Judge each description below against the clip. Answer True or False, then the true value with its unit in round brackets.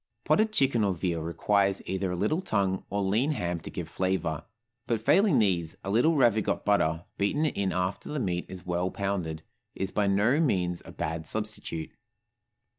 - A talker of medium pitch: False (100 Hz)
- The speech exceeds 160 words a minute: True (175 wpm)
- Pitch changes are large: False (3.9 semitones)